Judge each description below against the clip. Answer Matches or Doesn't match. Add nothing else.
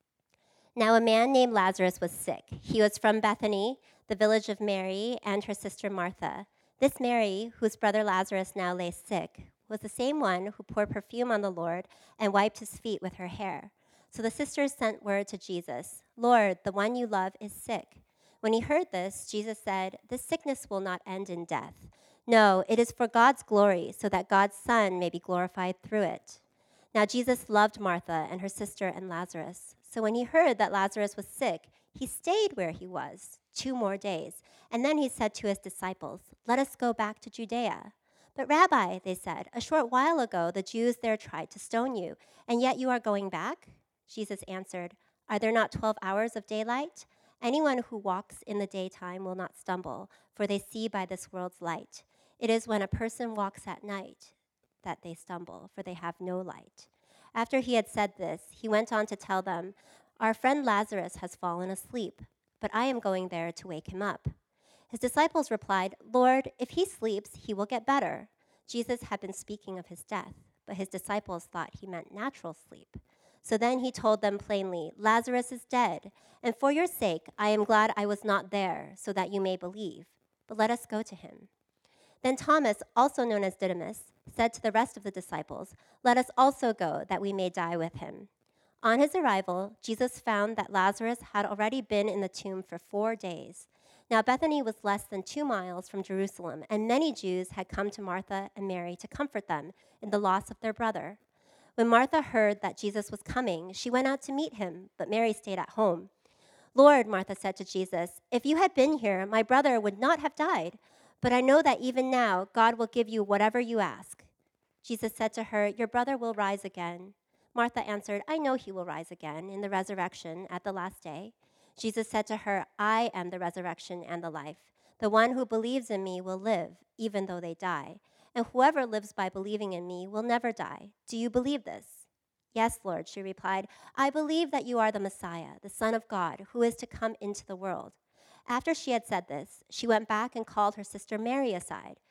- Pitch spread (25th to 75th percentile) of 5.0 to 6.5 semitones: Doesn't match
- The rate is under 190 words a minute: Doesn't match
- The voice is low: Doesn't match